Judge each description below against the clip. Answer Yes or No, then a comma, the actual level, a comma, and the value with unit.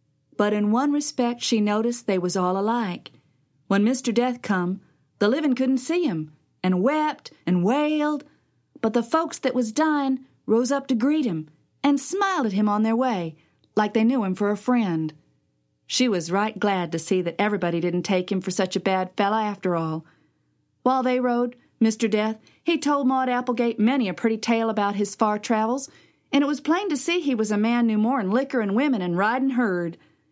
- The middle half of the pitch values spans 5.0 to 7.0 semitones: Yes, wide, 5.6 semitones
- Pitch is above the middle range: Yes, high, 225 Hz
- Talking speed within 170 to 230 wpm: Yes, average, 200 wpm